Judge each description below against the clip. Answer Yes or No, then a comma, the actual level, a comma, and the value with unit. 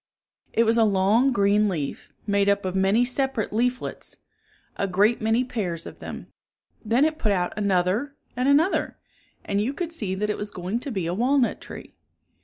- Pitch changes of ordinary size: Yes, average, 4.2 semitones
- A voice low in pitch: No, high, 210 Hz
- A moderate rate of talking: Yes, average, 185 wpm